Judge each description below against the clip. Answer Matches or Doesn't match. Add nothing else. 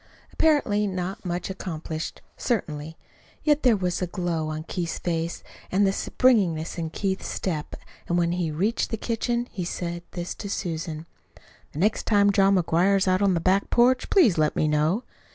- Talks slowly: Doesn't match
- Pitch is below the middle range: Doesn't match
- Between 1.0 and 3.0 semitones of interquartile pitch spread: Doesn't match